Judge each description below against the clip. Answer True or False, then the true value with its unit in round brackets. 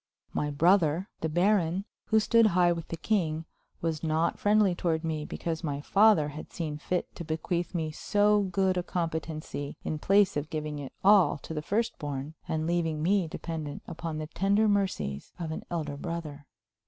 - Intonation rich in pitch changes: False (3.7 semitones)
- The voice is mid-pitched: True (165 Hz)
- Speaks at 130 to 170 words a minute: False (180 wpm)